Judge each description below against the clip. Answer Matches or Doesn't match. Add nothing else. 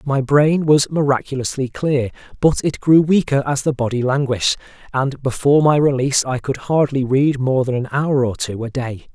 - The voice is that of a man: Matches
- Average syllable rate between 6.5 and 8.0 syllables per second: Doesn't match